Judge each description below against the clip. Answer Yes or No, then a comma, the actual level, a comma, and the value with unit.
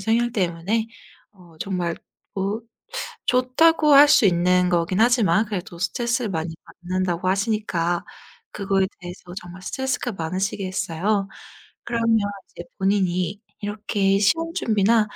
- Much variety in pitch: No, average, 3.9 semitones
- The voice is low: No, high, 195 Hz